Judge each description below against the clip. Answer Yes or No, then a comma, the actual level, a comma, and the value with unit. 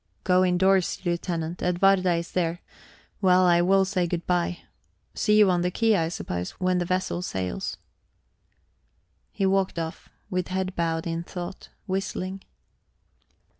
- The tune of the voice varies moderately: No, narrow, 1.6 semitones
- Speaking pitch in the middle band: Yes, medium, 180 Hz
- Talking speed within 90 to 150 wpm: Yes, average, 140 wpm